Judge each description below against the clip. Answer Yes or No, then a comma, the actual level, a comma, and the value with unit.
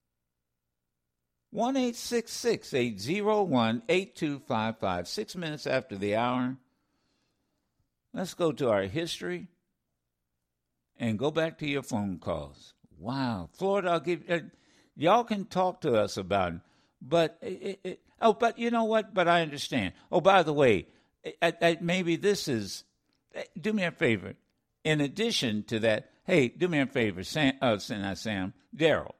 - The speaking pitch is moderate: Yes, medium, 150 Hz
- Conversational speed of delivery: Yes, average, 145 wpm